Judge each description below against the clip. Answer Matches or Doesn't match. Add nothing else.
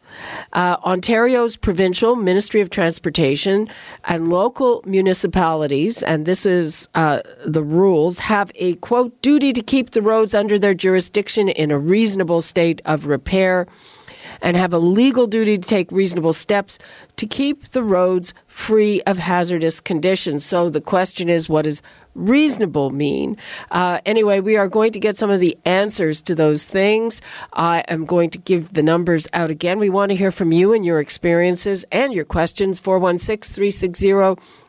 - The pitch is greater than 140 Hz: Matches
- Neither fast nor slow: Matches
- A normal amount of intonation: Matches